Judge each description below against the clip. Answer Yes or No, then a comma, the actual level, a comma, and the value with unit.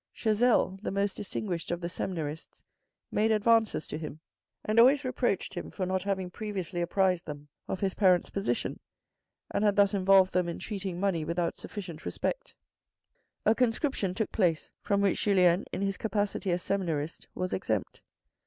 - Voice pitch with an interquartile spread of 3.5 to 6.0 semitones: No, average, 3.1 semitones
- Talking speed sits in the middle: Yes, average, 160 wpm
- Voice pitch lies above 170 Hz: Yes, high, 190 Hz